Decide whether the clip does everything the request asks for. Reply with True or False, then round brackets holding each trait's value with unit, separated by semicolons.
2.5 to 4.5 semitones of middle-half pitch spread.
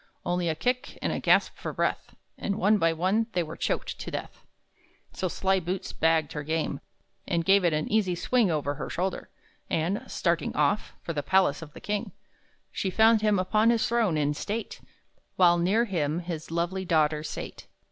True (4.0 semitones)